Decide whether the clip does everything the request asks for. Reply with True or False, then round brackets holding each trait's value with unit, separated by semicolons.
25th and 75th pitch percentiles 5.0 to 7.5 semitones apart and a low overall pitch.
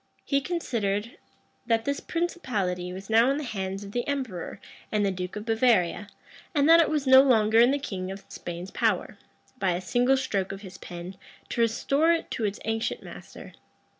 False (5.6 semitones; 225 Hz)